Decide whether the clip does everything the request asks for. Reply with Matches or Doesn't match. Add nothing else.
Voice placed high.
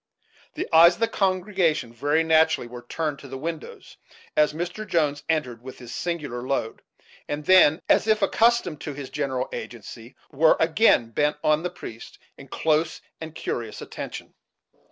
Doesn't match